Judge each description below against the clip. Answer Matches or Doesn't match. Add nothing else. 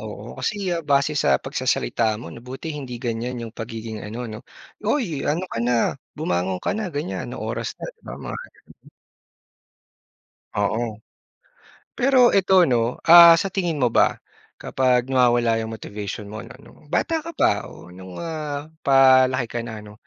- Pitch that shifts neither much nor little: Doesn't match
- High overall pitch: Doesn't match